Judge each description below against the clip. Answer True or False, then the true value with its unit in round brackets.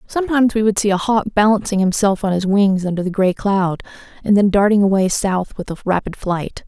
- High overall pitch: True (200 Hz)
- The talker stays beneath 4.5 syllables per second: False (5.5 syllables/s)